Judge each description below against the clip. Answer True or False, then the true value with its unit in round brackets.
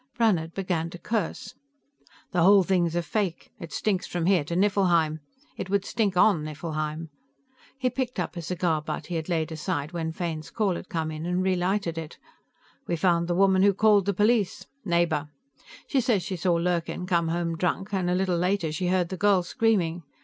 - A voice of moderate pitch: True (175 Hz)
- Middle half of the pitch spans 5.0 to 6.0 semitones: False (2.8 semitones)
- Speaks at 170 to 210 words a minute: True (195 wpm)